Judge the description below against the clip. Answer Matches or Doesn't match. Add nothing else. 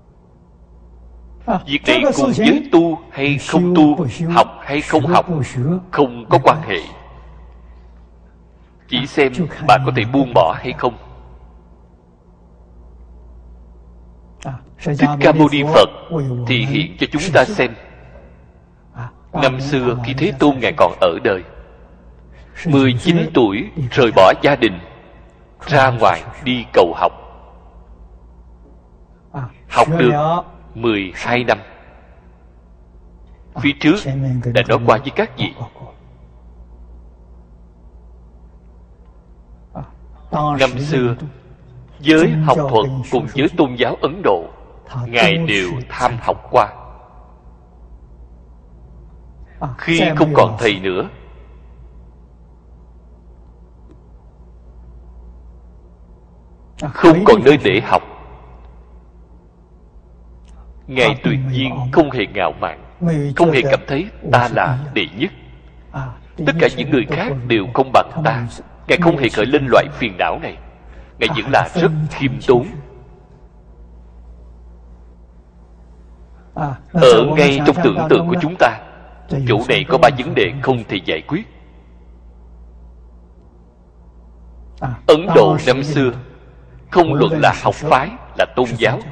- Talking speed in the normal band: Doesn't match